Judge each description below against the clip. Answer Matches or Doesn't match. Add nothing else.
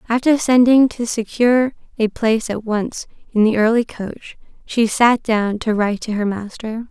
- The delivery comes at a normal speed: Matches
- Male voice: Doesn't match